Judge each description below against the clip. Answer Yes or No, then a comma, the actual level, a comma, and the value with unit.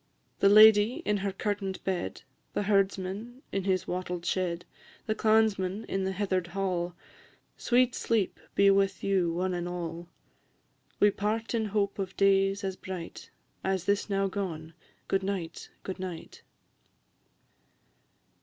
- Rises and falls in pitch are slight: Yes, narrow, 1.9 semitones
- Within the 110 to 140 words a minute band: Yes, slow, 135 wpm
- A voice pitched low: No, high, 195 Hz